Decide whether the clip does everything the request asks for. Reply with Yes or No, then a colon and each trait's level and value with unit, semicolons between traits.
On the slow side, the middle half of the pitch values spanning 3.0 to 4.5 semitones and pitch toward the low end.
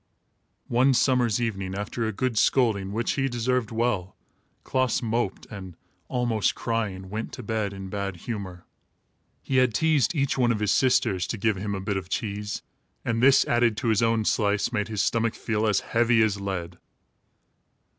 No: average, 175 wpm; average, 3.3 semitones; low, 110 Hz